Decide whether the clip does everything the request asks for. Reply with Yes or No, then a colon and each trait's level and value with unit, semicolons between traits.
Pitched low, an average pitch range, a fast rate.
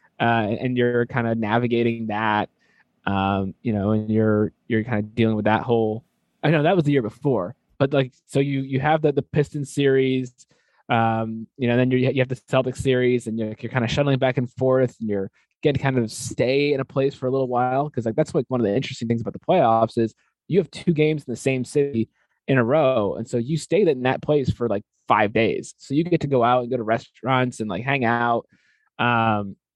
Yes: low, 125 Hz; average, 3.3 semitones; fast, 240 wpm